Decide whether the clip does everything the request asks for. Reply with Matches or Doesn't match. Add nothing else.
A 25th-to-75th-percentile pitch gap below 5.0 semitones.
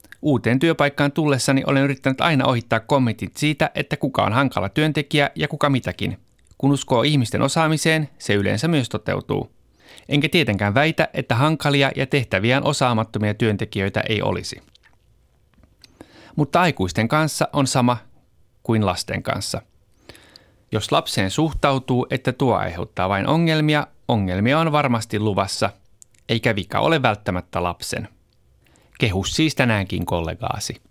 Doesn't match